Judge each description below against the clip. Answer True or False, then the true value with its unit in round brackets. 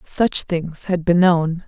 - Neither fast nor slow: True (180 wpm)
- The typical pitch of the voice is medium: True (175 Hz)